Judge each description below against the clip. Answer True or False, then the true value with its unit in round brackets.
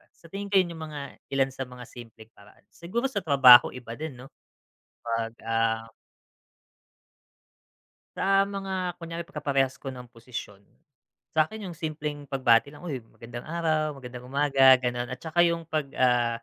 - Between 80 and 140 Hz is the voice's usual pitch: True (135 Hz)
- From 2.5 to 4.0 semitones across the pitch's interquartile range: False (5.4 semitones)